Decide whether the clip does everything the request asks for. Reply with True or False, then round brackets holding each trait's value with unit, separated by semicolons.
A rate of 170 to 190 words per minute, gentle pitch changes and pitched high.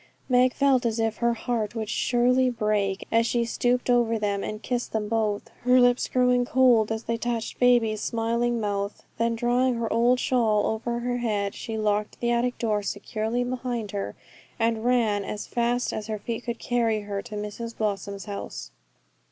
True (180 wpm; 2.3 semitones; 230 Hz)